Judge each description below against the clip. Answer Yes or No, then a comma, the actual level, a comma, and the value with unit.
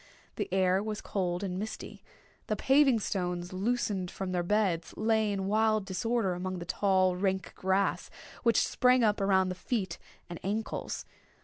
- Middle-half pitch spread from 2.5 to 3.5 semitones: Yes, average, 2.8 semitones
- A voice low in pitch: No, high, 195 Hz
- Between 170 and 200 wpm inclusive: No, average, 155 wpm